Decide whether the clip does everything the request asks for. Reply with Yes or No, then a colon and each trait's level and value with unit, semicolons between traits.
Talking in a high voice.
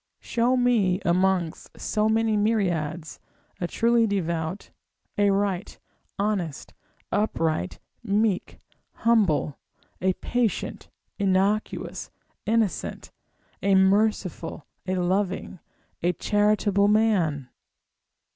Yes: high, 200 Hz